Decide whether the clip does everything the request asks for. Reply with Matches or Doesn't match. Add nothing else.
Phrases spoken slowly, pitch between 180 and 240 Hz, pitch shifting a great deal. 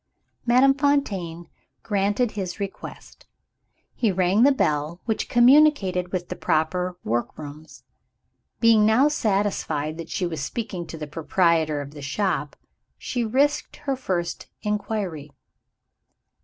Matches